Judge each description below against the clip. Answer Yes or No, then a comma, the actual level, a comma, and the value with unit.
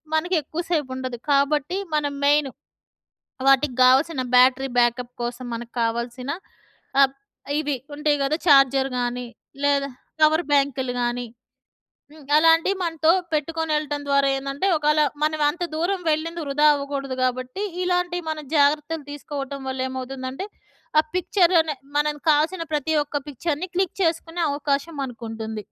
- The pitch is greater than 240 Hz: Yes, very high, 290 Hz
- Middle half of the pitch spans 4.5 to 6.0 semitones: No, average, 3.2 semitones